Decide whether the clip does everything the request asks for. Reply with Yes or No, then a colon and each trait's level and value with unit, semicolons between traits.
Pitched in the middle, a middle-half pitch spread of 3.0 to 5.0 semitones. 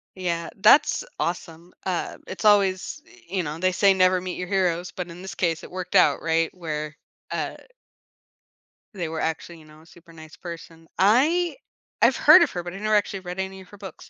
No: medium, 180 Hz; narrow, 2.5 semitones